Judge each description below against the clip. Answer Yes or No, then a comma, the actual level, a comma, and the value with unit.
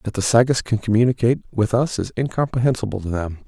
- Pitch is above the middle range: No, low, 115 Hz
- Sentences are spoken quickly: No, average, 190 wpm